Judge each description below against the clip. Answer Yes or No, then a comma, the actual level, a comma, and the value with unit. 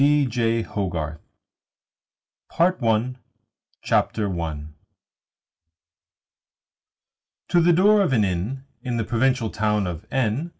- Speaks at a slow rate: Yes, slow, 100 wpm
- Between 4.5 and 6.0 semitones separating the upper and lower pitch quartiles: Yes, average, 5.1 semitones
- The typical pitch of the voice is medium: No, low, 115 Hz